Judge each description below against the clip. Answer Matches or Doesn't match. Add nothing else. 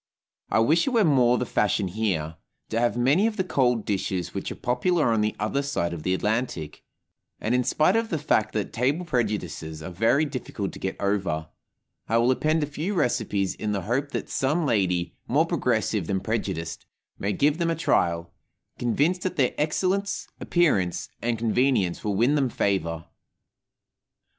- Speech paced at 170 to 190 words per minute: Matches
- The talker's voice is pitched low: Matches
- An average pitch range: Doesn't match